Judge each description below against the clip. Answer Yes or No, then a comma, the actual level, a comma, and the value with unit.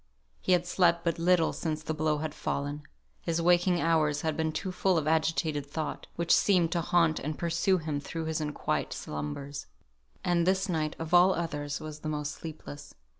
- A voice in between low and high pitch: Yes, medium, 160 Hz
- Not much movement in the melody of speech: Yes, narrow, 2.2 semitones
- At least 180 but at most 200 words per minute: Yes, average, 185 wpm